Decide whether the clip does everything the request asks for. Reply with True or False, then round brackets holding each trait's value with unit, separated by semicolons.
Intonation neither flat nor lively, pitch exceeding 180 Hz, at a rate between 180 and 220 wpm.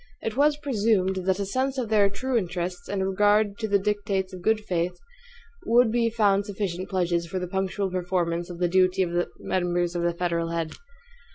True (3.0 semitones; 190 Hz; 200 wpm)